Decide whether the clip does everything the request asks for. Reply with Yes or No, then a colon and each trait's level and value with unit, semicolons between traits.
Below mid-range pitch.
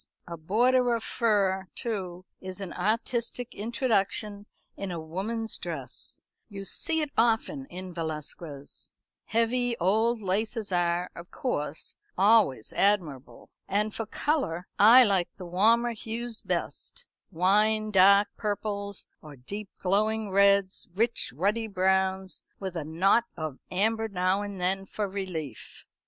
No: high, 200 Hz